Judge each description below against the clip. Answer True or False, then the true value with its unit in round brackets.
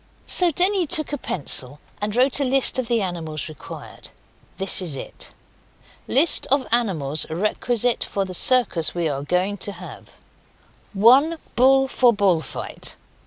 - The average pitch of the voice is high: True (210 Hz)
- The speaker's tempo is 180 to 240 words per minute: False (150 wpm)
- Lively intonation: True (7.1 semitones)